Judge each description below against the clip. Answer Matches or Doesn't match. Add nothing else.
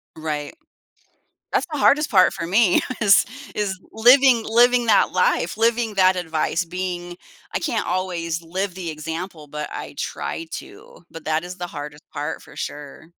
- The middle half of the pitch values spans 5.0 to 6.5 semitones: Matches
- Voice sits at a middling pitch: Matches